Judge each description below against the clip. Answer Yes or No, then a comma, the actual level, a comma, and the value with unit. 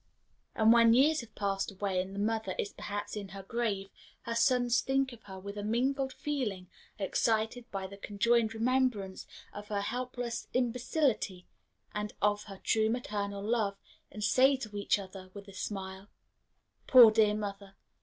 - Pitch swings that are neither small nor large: Yes, average, 3.3 semitones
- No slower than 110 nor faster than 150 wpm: No, average, 165 wpm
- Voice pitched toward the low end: No, high, 210 Hz